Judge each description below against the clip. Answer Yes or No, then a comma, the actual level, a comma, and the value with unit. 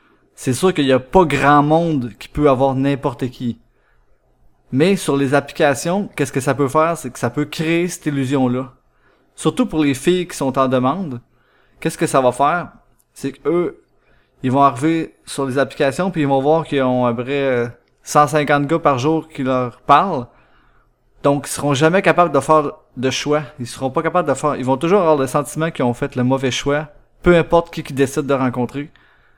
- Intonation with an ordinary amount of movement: Yes, average, 3.2 semitones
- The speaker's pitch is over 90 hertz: Yes, medium, 140 Hz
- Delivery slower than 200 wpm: No, average, 205 wpm